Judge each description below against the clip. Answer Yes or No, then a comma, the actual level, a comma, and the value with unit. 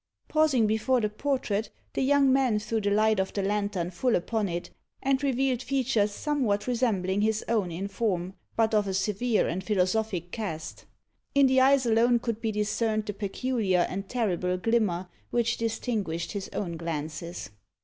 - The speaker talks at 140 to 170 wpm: Yes, average, 165 wpm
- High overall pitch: Yes, high, 215 Hz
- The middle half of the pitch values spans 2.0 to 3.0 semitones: No, average, 4.1 semitones